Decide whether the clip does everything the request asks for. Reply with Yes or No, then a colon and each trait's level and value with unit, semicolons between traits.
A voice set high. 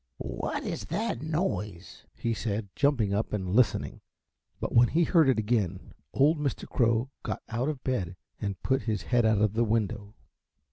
No: low, 115 Hz